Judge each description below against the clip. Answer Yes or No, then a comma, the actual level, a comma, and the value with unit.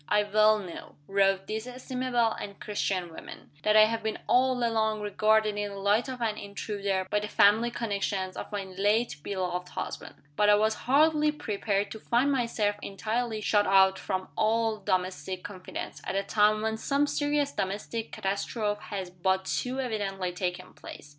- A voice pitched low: No, high, 210 Hz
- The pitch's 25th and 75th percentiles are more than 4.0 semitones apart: No, average, 2.7 semitones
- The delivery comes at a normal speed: Yes, average, 170 wpm